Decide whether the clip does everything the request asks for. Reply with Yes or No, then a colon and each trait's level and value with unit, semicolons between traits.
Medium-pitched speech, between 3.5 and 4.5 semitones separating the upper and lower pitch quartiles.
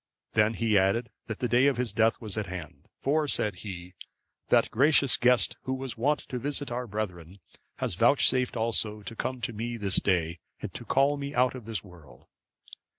No: low, 115 Hz; average, 4.0 semitones